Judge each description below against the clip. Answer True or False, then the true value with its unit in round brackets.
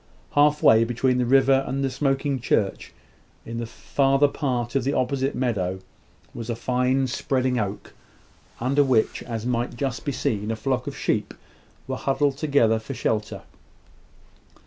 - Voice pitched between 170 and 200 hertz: False (130 Hz)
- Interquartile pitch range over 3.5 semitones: False (2.8 semitones)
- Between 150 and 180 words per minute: True (155 wpm)